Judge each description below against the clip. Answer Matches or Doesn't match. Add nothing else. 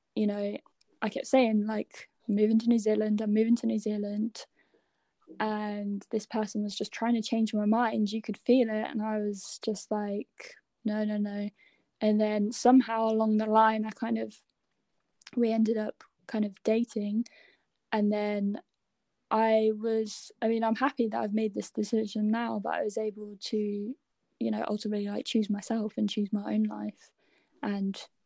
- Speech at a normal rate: Matches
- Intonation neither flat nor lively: Doesn't match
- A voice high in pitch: Matches